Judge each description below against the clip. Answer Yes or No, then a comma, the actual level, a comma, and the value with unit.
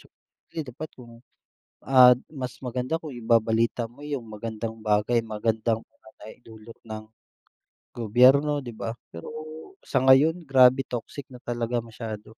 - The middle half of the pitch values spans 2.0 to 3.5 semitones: Yes, narrow, 2.5 semitones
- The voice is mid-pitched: No, low, 120 Hz